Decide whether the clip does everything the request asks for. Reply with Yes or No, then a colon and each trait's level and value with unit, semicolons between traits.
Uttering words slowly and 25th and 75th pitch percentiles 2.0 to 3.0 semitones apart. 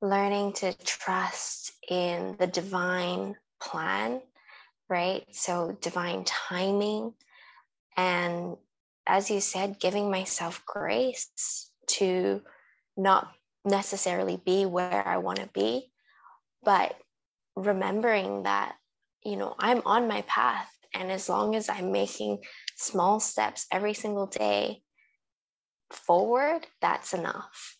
Yes: slow, 110 wpm; narrow, 2.5 semitones